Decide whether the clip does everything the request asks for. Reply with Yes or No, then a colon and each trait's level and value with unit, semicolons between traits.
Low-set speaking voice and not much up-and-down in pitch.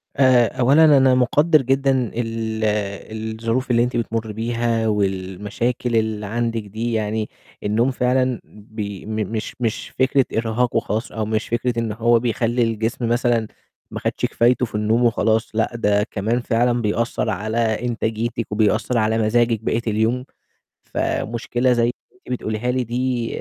Yes: low, 115 Hz; narrow, 1.9 semitones